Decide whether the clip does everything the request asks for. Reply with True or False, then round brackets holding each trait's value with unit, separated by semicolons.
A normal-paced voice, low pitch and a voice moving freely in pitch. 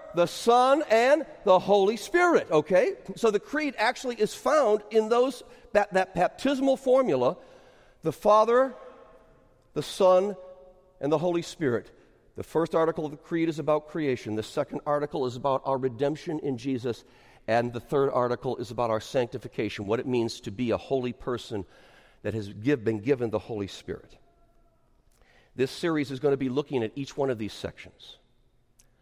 False (170 wpm; 150 Hz; 8.5 semitones)